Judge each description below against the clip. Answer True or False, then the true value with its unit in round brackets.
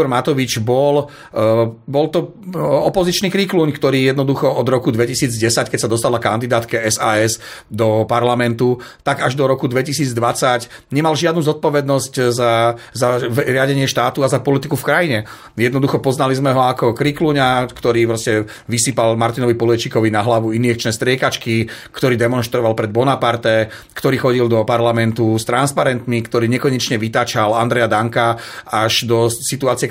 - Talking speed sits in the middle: True (140 wpm)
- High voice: False (120 Hz)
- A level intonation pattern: False (3.0 semitones)